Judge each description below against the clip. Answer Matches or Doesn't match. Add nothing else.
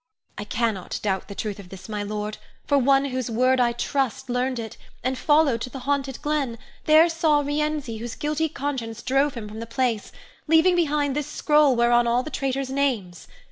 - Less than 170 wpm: Doesn't match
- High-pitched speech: Matches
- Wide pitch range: Doesn't match